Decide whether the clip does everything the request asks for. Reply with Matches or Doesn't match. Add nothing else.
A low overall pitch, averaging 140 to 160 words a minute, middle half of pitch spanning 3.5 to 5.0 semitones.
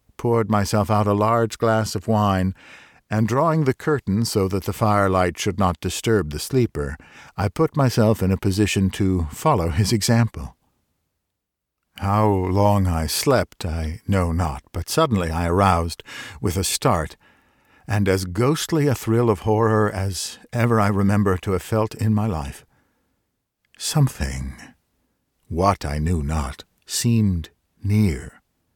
Matches